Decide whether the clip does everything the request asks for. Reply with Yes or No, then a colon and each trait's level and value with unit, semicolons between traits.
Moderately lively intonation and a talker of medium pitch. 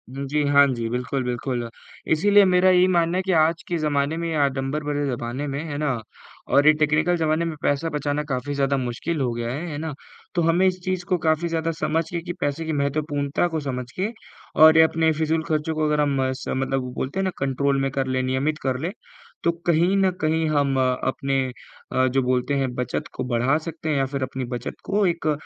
Yes: average, 3.3 semitones; medium, 150 Hz